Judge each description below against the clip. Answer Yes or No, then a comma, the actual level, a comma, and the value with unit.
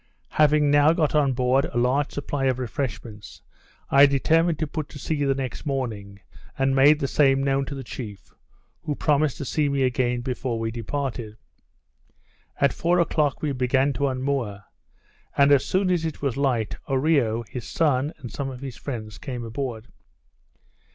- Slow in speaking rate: No, average, 170 wpm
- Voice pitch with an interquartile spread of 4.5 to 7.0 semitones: No, average, 2.9 semitones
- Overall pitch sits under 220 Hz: Yes, low, 135 Hz